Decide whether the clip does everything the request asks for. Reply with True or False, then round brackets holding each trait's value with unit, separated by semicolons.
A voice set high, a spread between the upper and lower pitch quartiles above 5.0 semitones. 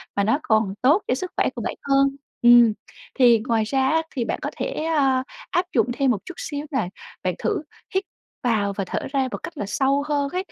False (265 Hz; 4.0 semitones)